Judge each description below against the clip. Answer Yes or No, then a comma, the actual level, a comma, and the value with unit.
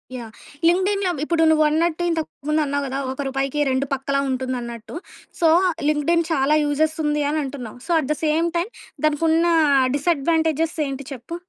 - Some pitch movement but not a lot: Yes, average, 3.2 semitones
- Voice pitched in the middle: No, very high, 300 Hz